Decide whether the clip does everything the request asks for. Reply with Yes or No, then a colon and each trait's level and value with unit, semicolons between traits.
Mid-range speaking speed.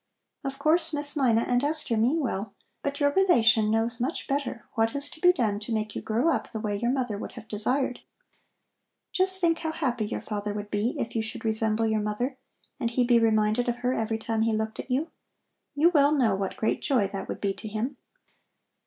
No: fast, 215 wpm